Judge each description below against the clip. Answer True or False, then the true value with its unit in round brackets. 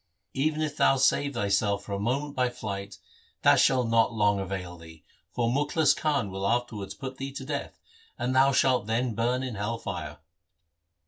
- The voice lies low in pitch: True (120 Hz)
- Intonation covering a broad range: False (4.9 semitones)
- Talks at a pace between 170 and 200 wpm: True (180 wpm)